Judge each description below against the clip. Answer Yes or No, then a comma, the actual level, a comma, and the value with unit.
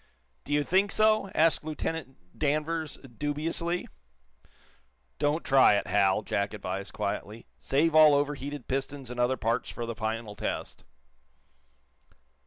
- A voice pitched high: No, medium, 140 Hz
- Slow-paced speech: Yes, slow, 125 wpm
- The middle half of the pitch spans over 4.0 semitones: Yes, wide, 5.4 semitones